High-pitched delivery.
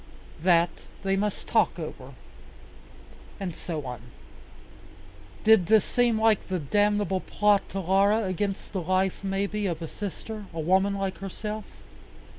Yes: high, 195 Hz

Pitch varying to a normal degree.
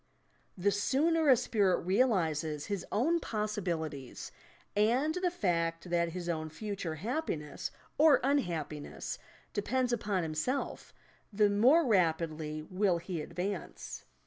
No: wide, 6.6 semitones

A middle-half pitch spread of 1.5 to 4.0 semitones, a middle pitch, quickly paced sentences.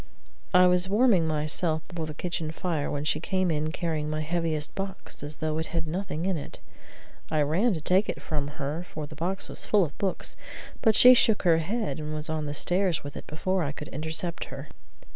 Yes: average, 3.2 semitones; medium, 160 Hz; fast, 215 wpm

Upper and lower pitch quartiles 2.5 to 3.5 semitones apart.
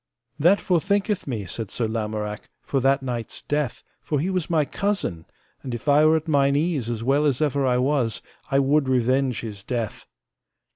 No: average, 4.5 semitones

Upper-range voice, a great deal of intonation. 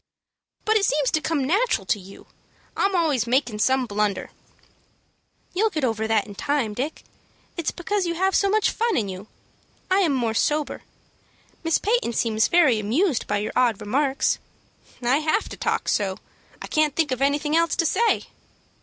Yes: very high, 285 Hz; wide, 7.2 semitones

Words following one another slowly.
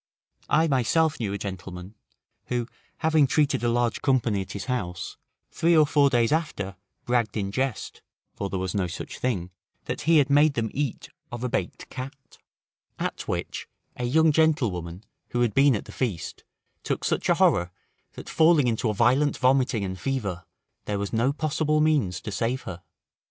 No: average, 180 wpm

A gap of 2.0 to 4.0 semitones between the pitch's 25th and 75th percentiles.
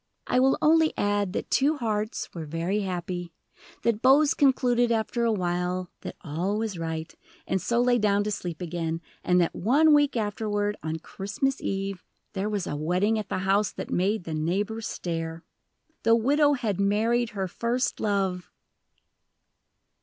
No: average, 4.7 semitones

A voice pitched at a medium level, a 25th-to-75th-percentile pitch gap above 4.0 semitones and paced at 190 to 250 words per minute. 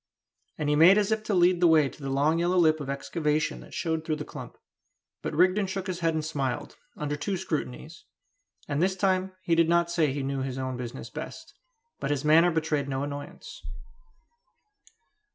No: medium, 160 Hz; average, 3.5 semitones; average, 200 wpm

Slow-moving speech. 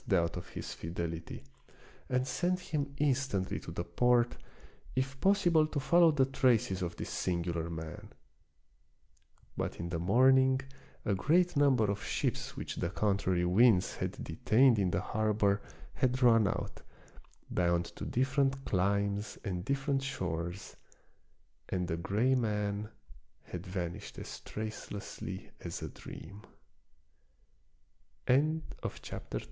Yes: slow, 120 wpm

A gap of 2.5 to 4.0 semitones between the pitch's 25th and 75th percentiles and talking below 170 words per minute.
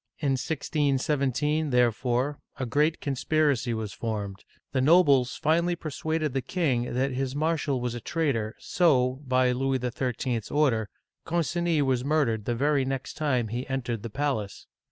Yes: average, 3.5 semitones; average, 150 wpm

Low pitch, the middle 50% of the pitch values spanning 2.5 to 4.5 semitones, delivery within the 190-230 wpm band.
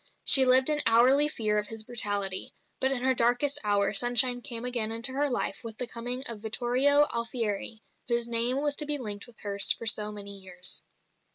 No: high, 235 Hz; average, 3.4 semitones; average, 195 wpm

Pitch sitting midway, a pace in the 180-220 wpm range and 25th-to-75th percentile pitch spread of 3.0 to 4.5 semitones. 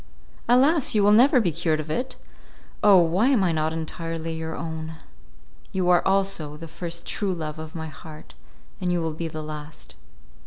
Yes: medium, 165 Hz; average, 185 wpm; average, 3.5 semitones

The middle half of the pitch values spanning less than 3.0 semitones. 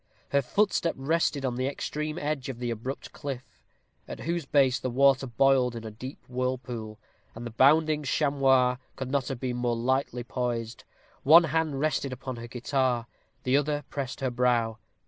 Yes: narrow, 2.5 semitones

